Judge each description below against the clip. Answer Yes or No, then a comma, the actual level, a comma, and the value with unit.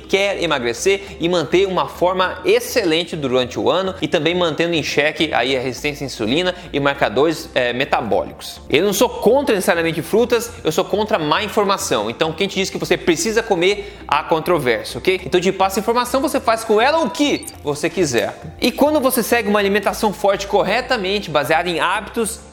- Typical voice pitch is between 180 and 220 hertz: Yes, high, 190 Hz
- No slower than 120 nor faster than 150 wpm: No, fast, 185 wpm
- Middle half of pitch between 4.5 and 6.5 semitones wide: Yes, wide, 5.6 semitones